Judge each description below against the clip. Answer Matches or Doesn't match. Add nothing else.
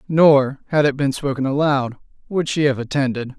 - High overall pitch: Doesn't match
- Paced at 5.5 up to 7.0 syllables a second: Doesn't match